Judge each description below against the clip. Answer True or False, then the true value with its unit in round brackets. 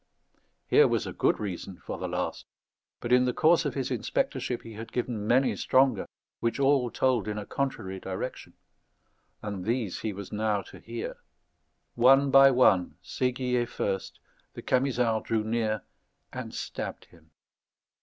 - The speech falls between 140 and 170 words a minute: True (155 wpm)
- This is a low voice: True (115 Hz)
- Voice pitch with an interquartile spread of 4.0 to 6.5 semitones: False (3.5 semitones)